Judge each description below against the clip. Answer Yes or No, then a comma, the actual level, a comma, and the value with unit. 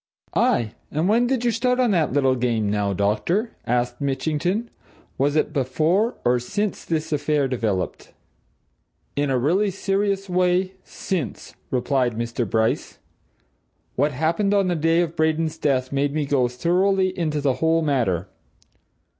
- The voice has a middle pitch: Yes, medium, 155 Hz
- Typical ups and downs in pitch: No, wide, 6.4 semitones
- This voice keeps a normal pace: Yes, average, 145 wpm